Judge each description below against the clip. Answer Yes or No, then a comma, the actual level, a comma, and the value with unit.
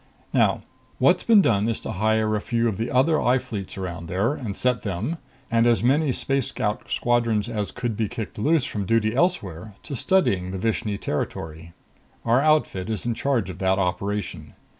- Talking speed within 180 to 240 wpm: Yes, average, 185 wpm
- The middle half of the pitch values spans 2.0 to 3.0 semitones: No, average, 4.1 semitones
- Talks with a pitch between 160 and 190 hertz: No, low, 110 Hz